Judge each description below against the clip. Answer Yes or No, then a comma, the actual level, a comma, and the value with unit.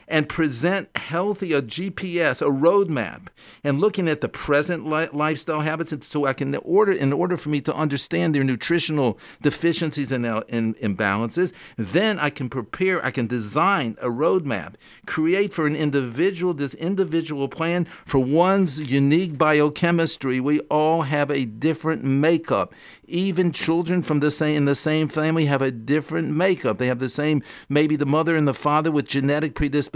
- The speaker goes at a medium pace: Yes, average, 165 wpm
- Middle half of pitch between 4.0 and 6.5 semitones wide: No, average, 3.1 semitones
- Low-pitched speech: No, medium, 150 Hz